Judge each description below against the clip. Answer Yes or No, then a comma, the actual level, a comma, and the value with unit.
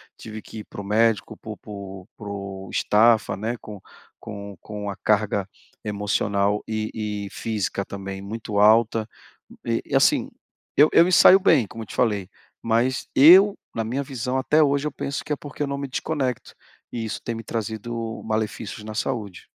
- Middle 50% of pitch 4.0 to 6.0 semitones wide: No, average, 3.5 semitones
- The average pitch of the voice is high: No, low, 110 Hz